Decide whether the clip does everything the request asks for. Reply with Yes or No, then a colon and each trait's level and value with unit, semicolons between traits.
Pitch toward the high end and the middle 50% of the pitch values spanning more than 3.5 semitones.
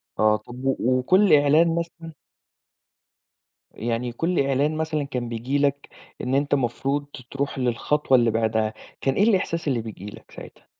No: low, 135 Hz; average, 4.2 semitones